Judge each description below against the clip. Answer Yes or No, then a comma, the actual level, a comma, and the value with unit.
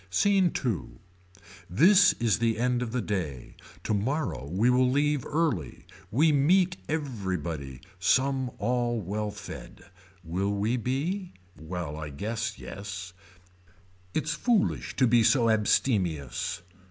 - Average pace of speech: No, slow, 120 wpm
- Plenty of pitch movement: Yes, wide, 6.9 semitones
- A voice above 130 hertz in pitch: No, low, 115 Hz